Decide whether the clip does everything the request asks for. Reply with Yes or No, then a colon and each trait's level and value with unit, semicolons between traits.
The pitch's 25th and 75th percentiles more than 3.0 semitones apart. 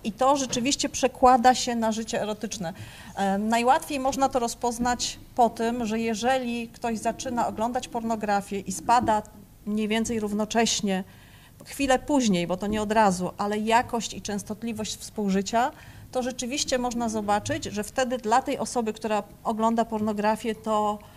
No: average, 2.7 semitones